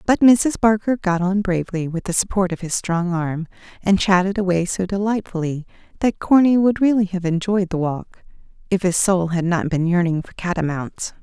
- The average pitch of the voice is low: No, medium, 185 Hz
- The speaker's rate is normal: Yes, average, 185 wpm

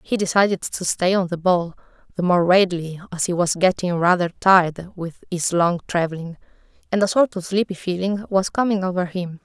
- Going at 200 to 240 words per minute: No, average, 190 wpm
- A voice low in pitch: No, medium, 185 Hz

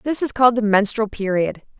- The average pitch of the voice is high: Yes, high, 220 Hz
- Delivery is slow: No, average, 200 wpm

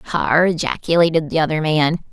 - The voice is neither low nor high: Yes, medium, 160 Hz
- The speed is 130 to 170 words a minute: Yes, average, 140 wpm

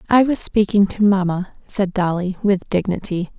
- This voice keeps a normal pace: Yes, average, 160 wpm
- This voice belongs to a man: No, female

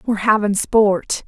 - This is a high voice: Yes, high, 210 Hz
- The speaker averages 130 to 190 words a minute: Yes, average, 140 wpm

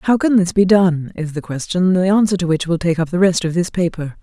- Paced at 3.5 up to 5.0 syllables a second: No, 5.6 syllables/s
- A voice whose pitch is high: No, medium, 175 Hz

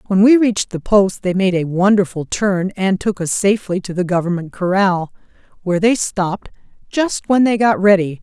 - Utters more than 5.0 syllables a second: Yes, 5.2 syllables/s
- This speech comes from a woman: Yes, female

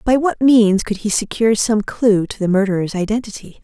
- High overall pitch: Yes, high, 215 Hz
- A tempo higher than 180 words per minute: Yes, average, 200 wpm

